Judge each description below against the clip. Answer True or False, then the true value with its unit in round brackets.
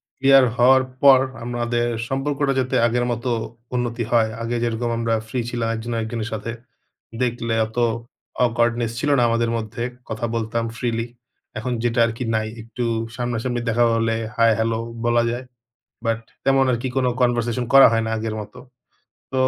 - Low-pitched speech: True (120 Hz)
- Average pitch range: False (1.4 semitones)